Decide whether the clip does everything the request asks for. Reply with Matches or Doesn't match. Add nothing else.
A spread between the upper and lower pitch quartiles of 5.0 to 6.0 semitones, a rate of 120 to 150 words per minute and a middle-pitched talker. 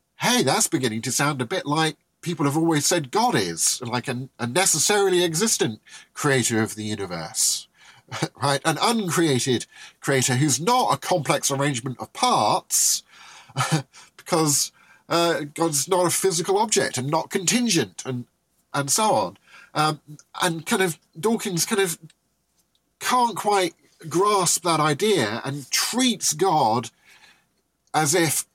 Matches